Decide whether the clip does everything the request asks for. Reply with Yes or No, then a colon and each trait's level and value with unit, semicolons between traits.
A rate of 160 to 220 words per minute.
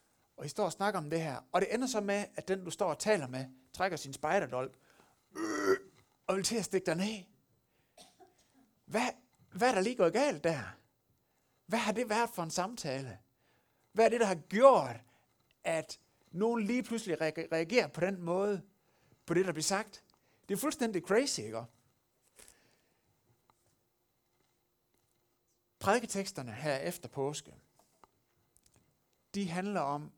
No: average, 150 wpm